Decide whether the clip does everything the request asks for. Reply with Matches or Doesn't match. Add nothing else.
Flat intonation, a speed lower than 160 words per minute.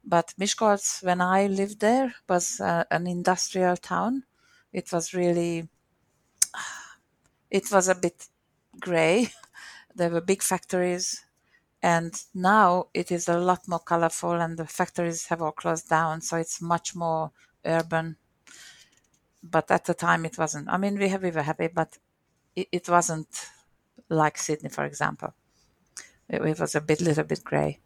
Matches